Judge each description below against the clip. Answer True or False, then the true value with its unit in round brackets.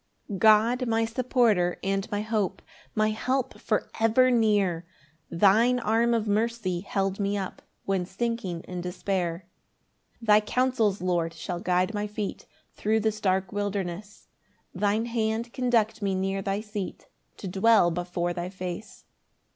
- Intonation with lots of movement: False (3.2 semitones)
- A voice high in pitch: True (205 Hz)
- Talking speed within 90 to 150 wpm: True (145 wpm)